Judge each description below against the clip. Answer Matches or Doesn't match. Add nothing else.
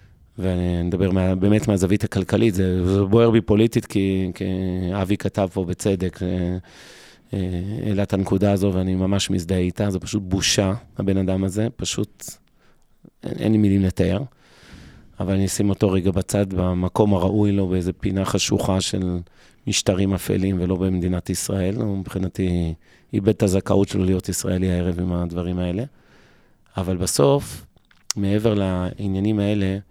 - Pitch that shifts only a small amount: Matches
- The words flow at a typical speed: Matches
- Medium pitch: Doesn't match